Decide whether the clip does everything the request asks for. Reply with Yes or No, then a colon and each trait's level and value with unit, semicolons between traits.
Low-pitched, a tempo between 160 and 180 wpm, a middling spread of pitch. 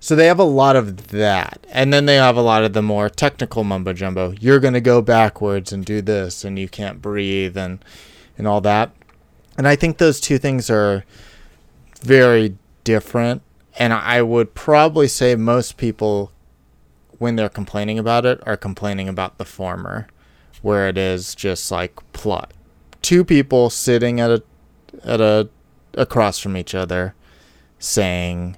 Yes: low, 105 Hz; average, 165 wpm; average, 4.2 semitones